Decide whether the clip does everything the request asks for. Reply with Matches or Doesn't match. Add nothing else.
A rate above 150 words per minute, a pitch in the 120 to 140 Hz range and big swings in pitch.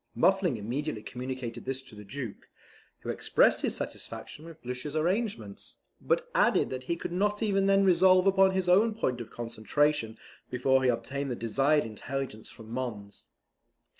Matches